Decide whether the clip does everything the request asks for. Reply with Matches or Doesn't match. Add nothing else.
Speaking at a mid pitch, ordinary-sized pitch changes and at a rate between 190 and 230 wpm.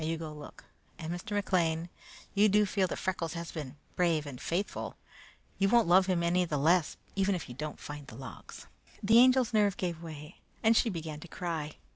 Matches